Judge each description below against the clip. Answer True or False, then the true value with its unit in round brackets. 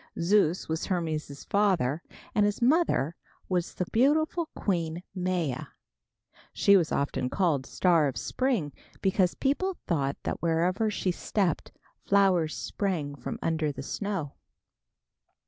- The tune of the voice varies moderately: True (4.4 semitones)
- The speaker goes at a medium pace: False (125 wpm)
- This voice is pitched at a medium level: True (180 Hz)